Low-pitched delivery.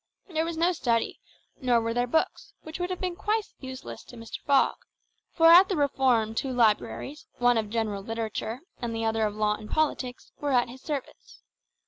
No: high, 245 Hz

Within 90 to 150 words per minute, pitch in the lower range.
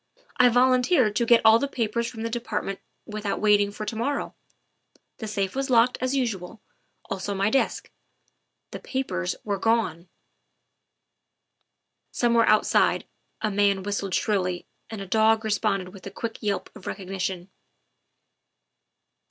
No: average, 140 wpm; high, 215 Hz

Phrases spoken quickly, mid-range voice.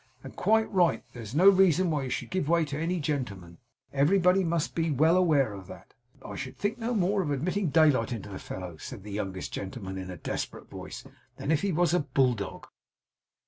Yes: fast, 210 wpm; medium, 150 Hz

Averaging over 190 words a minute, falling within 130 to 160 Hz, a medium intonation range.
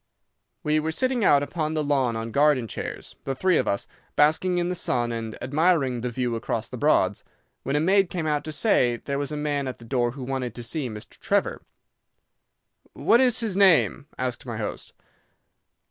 Yes: average, 200 wpm; medium, 140 Hz; average, 4.8 semitones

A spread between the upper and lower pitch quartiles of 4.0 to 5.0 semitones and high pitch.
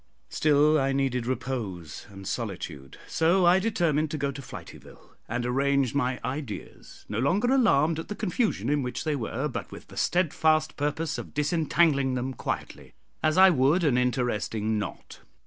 No: average, 4.3 semitones; medium, 140 Hz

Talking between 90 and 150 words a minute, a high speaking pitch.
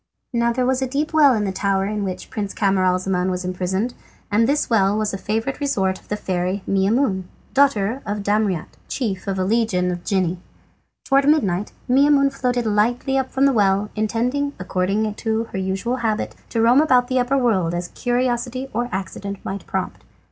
No: average, 185 wpm; high, 215 Hz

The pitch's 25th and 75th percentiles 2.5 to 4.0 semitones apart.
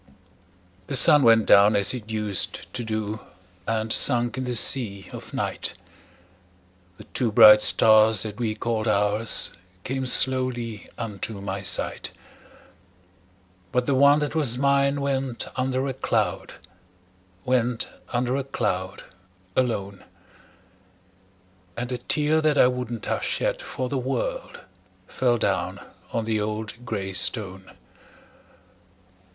Yes: average, 3.3 semitones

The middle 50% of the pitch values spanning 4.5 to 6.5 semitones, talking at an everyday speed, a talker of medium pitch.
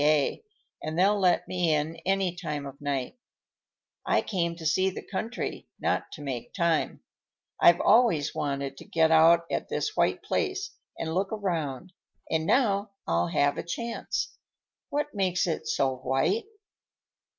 Yes: average, 4.9 semitones; average, 150 wpm; medium, 170 Hz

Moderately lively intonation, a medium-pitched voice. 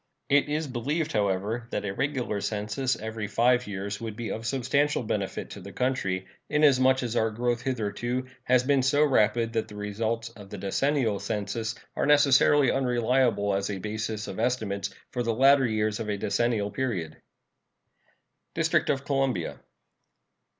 No: average, 4.1 semitones; low, 115 Hz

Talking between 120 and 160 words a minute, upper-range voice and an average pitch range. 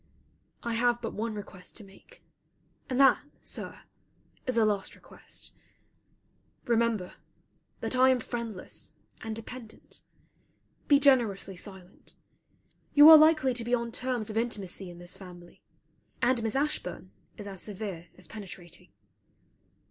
Yes: slow, 135 wpm; high, 225 Hz; average, 4.3 semitones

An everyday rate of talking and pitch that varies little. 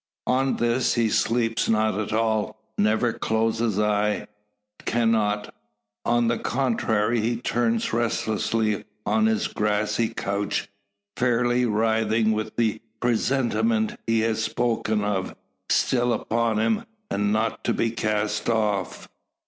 No: slow, 120 wpm; narrow, 1.8 semitones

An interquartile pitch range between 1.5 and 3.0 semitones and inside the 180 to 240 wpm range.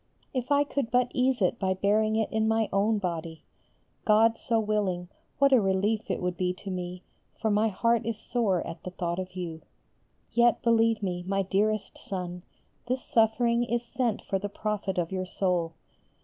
No: average, 3.8 semitones; average, 185 wpm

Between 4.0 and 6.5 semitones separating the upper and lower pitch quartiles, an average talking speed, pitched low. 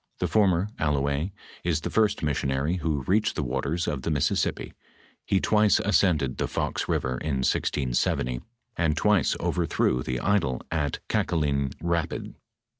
Yes: average, 4.6 semitones; average, 145 wpm; very low, 75 Hz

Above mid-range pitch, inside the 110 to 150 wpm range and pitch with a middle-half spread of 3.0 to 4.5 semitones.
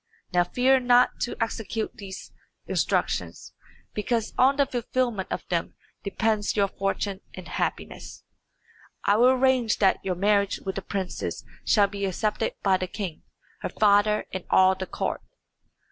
Yes: high, 205 Hz; average, 145 wpm; average, 3.5 semitones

